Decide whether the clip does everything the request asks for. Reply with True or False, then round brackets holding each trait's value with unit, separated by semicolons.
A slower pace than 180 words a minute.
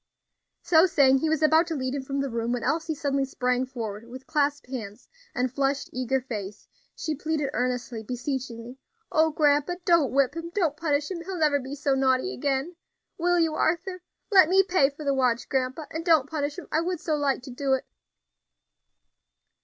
False (195 wpm)